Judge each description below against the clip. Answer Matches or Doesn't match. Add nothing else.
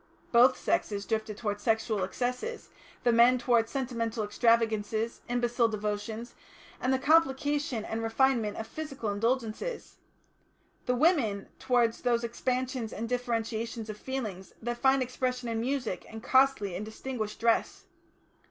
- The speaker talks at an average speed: Doesn't match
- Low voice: Doesn't match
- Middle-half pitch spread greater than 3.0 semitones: Doesn't match